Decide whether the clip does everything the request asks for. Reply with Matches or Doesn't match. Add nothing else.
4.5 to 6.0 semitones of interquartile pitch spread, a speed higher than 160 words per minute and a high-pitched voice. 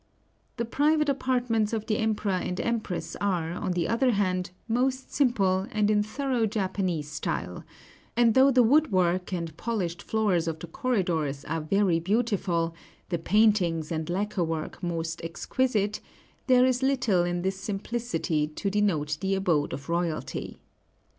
Doesn't match